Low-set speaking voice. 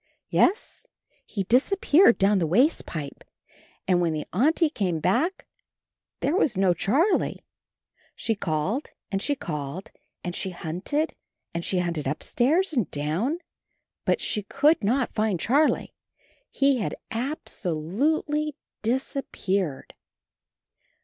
No: high, 215 Hz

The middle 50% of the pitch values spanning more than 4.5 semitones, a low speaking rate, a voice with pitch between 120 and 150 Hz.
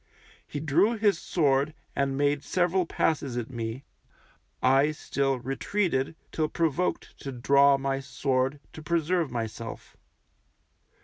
No: average, 3.3 semitones; slow, 120 wpm; medium, 140 Hz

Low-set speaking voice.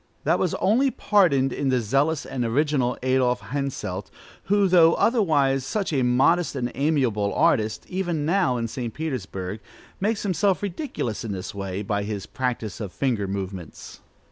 Yes: low, 130 Hz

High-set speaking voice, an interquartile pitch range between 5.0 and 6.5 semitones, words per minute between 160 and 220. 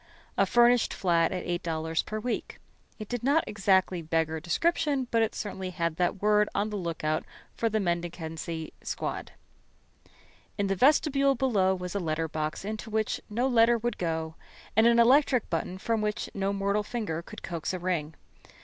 Yes: high, 195 Hz; wide, 5.4 semitones; average, 170 wpm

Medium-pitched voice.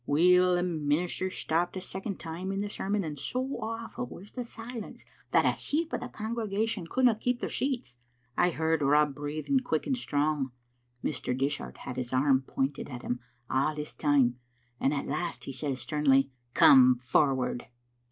Yes: medium, 155 Hz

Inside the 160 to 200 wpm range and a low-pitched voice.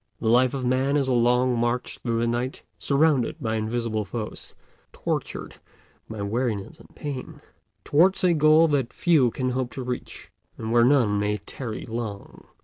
Yes: average, 165 wpm; low, 125 Hz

